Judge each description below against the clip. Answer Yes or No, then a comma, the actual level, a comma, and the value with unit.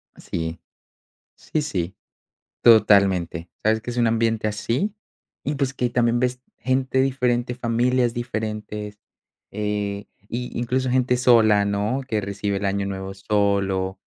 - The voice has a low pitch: Yes, low, 110 Hz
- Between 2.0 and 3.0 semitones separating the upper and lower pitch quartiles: No, average, 3.5 semitones